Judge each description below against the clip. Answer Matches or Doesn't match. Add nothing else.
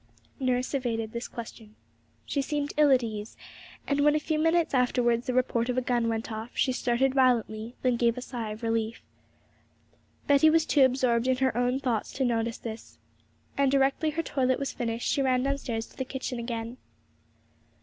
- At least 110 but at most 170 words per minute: Doesn't match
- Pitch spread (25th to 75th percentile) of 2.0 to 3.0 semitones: Matches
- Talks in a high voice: Matches